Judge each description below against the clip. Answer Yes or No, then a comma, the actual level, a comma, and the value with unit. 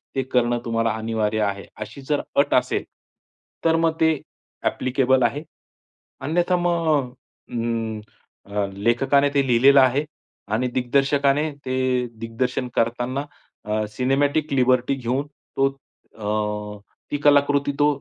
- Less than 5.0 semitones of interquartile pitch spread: Yes, average, 3.8 semitones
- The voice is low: Yes, low, 130 Hz